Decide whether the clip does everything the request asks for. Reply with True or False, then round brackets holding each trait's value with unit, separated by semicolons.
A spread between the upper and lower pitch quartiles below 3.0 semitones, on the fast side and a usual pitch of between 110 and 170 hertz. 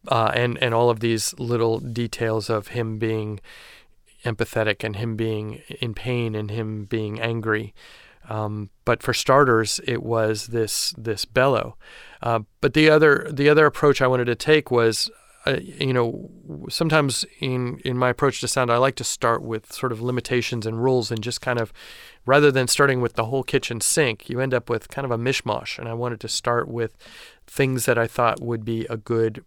False (2.4 semitones; 195 wpm; 120 Hz)